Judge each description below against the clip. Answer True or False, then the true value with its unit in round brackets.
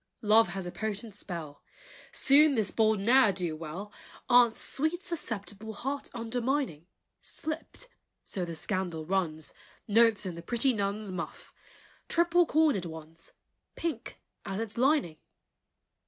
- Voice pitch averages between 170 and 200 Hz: False (215 Hz)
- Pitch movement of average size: False (6.6 semitones)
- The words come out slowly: True (125 wpm)